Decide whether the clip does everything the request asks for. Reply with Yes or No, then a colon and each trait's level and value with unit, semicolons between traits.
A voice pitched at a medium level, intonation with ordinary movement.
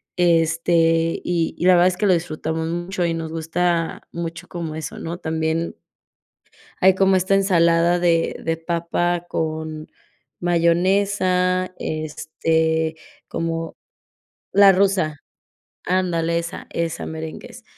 No: medium, 170 Hz; narrow, 1.7 semitones